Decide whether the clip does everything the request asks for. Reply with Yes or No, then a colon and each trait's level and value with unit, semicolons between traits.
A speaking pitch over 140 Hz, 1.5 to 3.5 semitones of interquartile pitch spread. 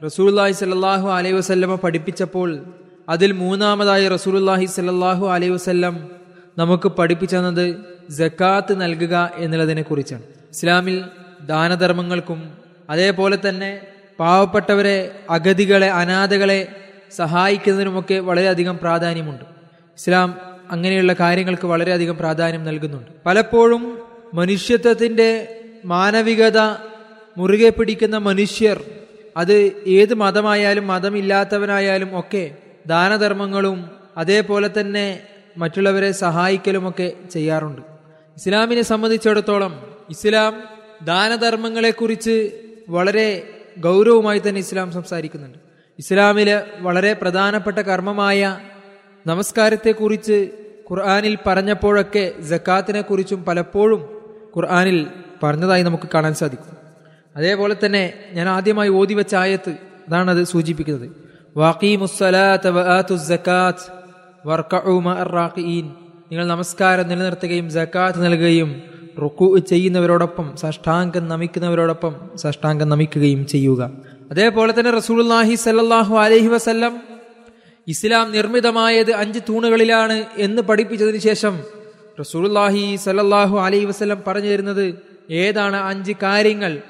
Yes: high, 190 Hz; average, 3.0 semitones